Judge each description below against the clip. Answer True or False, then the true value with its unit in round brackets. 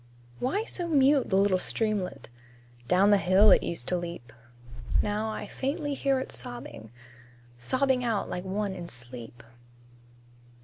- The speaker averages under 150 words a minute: True (140 wpm)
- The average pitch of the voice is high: True (200 Hz)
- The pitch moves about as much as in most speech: False (7.1 semitones)